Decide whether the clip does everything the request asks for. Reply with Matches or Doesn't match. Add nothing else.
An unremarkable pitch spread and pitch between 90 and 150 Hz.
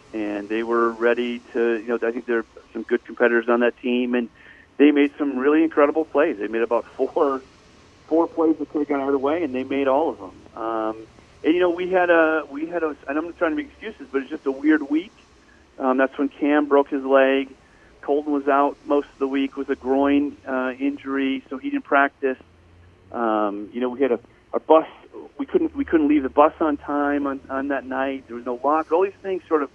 Matches